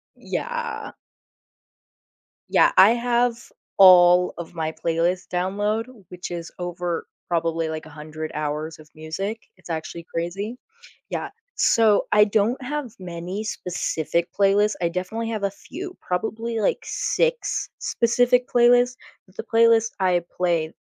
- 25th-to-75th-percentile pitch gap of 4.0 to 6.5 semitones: Yes, average, 5.2 semitones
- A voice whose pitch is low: No, high, 190 Hz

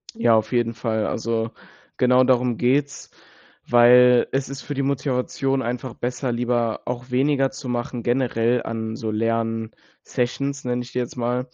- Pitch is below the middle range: Yes, low, 125 Hz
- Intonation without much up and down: Yes, narrow, 2.0 semitones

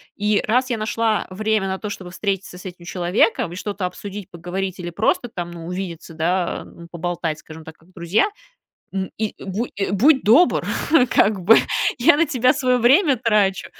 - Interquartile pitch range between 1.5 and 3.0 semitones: No, average, 4.1 semitones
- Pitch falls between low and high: No, high, 195 Hz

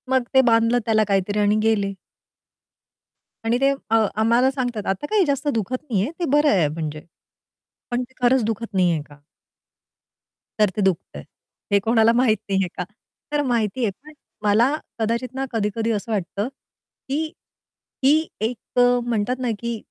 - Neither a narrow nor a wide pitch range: Yes, average, 3.7 semitones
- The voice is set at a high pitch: Yes, high, 225 Hz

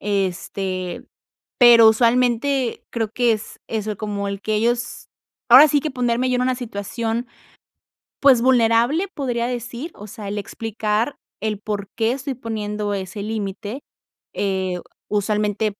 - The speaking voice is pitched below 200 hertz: No, high, 225 Hz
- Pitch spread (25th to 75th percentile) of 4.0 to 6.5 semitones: No, average, 3.0 semitones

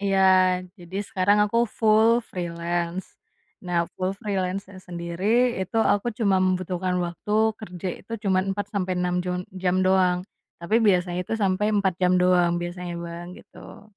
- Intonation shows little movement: Yes, narrow, 1.9 semitones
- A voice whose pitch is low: No, medium, 185 Hz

